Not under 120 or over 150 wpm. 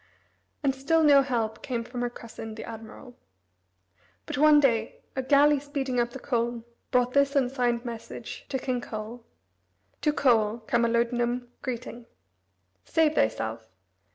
Yes: slow, 135 wpm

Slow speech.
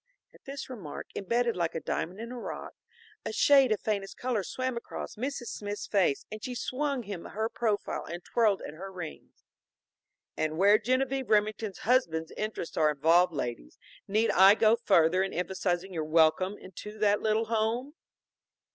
No: average, 165 wpm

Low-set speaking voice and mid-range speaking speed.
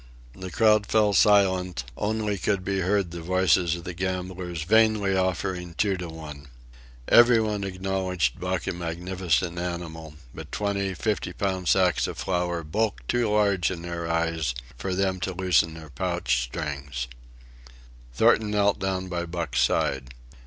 Yes: very low, 90 Hz; average, 145 wpm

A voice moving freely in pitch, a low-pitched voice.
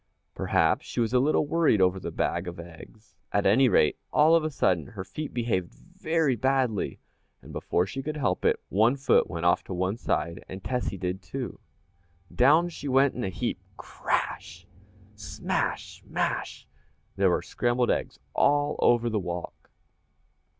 Yes: wide, 7.0 semitones; low, 120 Hz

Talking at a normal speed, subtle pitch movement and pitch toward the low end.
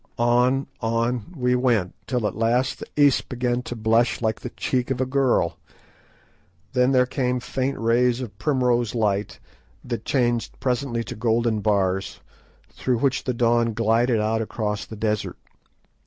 Yes: average, 155 wpm; narrow, 2.1 semitones; low, 120 Hz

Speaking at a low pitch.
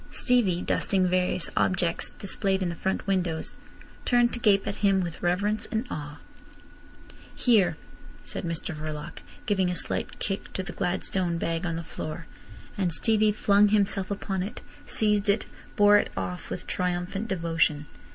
No: high, 190 Hz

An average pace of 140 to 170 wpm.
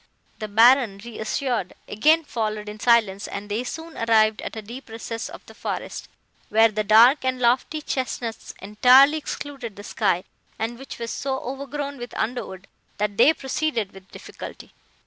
Yes: average, 160 wpm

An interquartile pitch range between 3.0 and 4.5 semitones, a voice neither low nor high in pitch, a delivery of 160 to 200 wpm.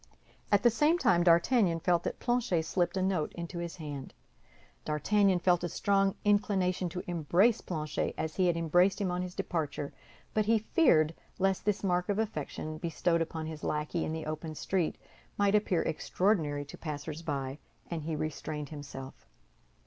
Yes: average, 3.8 semitones; medium, 170 Hz; average, 170 wpm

